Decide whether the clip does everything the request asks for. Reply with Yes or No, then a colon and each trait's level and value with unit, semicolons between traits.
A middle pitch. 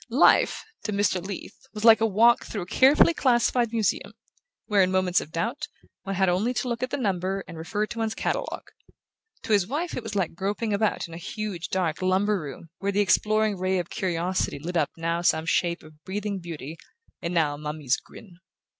No: high, 195 Hz